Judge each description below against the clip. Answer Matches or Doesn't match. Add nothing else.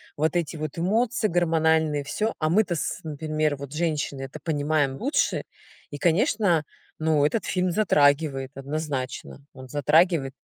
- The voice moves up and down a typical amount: Matches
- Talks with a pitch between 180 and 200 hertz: Doesn't match